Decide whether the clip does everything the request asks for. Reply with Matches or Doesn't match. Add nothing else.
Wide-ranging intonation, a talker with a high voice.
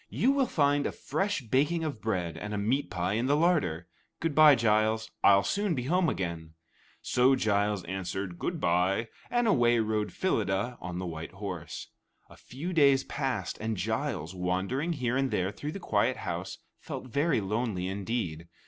Doesn't match